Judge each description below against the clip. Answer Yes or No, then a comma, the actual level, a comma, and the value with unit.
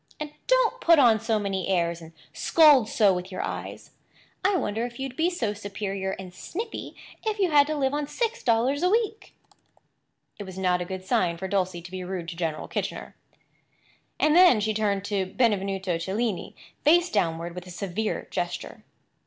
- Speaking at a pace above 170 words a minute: Yes, average, 180 wpm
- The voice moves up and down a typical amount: No, wide, 7.8 semitones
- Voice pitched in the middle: No, high, 205 Hz